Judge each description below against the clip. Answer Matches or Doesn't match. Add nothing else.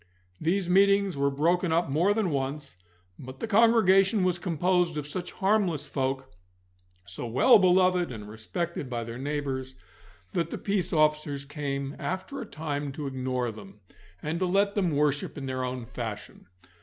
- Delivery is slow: Doesn't match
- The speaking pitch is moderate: Matches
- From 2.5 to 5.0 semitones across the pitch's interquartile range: Doesn't match